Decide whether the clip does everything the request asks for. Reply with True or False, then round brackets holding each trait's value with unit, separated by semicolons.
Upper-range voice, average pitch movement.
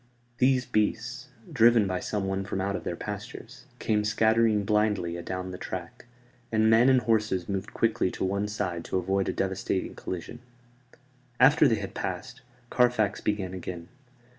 False (105 Hz; 3.3 semitones)